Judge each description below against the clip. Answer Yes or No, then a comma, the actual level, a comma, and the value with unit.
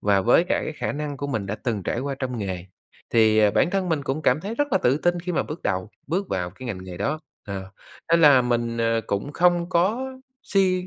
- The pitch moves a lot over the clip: Yes, wide, 8.2 semitones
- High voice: No, low, 135 Hz